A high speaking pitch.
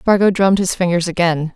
No: medium, 180 Hz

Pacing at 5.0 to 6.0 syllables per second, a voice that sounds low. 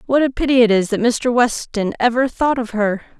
No: 5.3 syllables/s; high, 235 Hz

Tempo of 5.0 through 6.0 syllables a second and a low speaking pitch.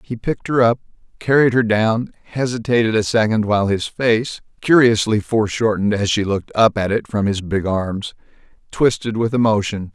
Yes: 5.3 syllables/s; low, 110 Hz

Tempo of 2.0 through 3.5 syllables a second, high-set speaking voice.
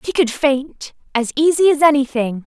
No: 4.7 syllables/s; very high, 275 Hz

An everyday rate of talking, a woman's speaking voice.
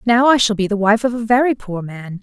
No: fast, 295 wpm; female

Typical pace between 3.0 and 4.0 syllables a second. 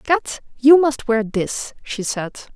Yes: 3.2 syllables/s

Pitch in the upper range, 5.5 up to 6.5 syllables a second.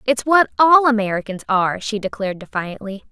Yes: high, 220 Hz; 5.7 syllables/s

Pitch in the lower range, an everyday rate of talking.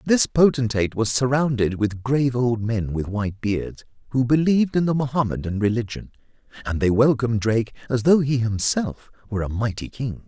Yes: low, 120 Hz; average, 170 wpm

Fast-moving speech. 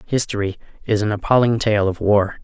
No: average, 175 wpm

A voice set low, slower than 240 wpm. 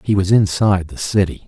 Yes: very low, 95 Hz; fast, 205 wpm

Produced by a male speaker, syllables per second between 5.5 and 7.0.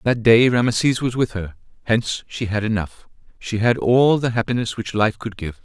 No: male; 5.1 syllables/s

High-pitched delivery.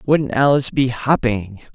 No: low, 125 Hz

